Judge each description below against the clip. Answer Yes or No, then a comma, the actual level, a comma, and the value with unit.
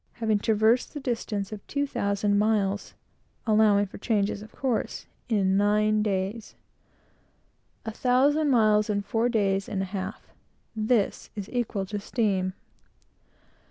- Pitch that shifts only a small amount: Yes, narrow, 2.1 semitones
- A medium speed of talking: No, slow, 130 wpm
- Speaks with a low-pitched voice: No, high, 210 Hz